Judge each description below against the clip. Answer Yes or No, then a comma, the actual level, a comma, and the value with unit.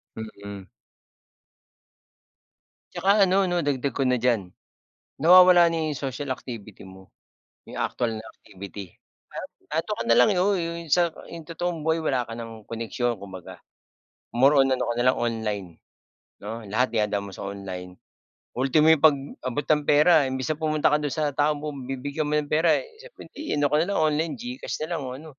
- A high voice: No, medium, 140 Hz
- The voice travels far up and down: Yes, wide, 5.9 semitones